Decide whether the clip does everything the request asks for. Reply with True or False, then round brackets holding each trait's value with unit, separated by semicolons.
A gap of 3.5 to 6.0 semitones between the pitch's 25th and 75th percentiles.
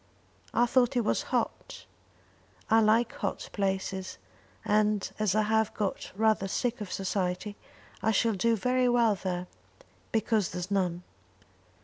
False (2.9 semitones)